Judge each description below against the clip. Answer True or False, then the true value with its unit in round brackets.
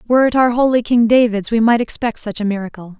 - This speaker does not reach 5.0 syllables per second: False (6.3 syllables/s)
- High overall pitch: True (230 Hz)